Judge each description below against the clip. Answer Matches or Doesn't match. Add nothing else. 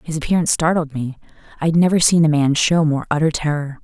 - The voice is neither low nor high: Matches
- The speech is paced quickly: Matches